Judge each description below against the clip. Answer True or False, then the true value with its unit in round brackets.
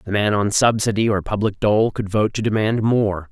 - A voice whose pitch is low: True (105 Hz)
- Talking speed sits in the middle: False (215 wpm)